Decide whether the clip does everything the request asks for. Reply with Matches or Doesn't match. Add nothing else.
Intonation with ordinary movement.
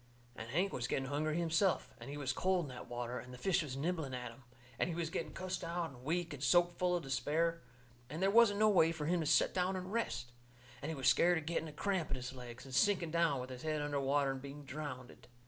Matches